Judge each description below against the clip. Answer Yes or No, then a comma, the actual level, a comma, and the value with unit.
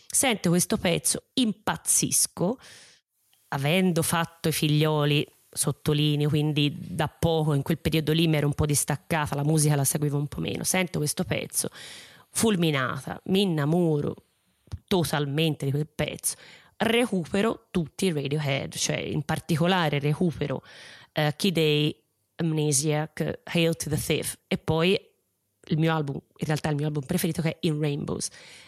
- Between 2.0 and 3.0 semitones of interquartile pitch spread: Yes, average, 2.7 semitones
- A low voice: No, medium, 155 Hz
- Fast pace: No, average, 145 wpm